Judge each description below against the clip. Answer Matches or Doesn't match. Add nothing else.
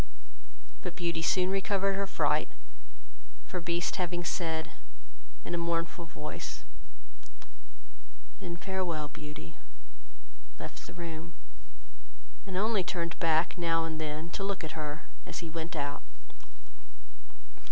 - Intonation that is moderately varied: Doesn't match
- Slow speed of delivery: Matches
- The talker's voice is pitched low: Doesn't match